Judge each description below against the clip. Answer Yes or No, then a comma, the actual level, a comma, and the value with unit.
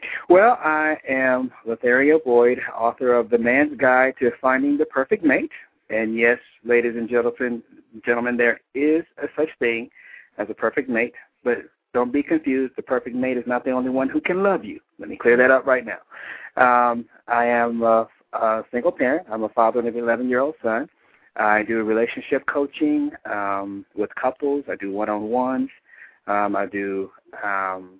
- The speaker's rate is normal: Yes, average, 185 wpm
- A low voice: Yes, low, 125 Hz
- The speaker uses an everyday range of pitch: Yes, average, 3.4 semitones